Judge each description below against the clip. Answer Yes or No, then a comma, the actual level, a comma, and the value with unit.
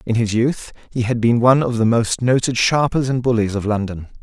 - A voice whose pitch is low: Yes, low, 120 Hz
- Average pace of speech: No, fast, 225 wpm